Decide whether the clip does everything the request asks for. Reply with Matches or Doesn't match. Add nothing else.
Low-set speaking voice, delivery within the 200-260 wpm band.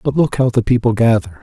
Matches